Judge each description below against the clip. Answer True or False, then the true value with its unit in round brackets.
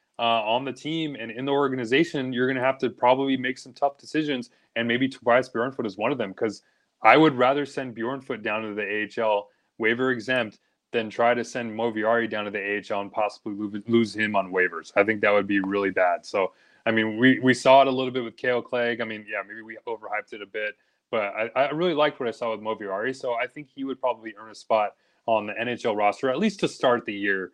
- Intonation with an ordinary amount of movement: True (3.3 semitones)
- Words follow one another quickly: True (245 wpm)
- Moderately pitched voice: False (115 Hz)